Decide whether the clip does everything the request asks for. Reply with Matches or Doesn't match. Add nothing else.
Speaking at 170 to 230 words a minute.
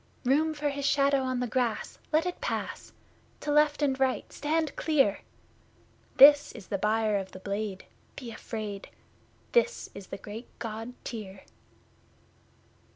Doesn't match